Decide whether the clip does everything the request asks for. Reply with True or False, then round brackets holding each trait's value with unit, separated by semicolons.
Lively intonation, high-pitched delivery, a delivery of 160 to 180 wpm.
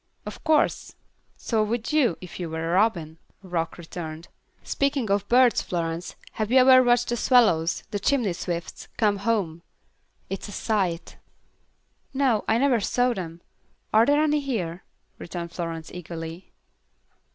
False (6.2 semitones; 200 Hz; 145 wpm)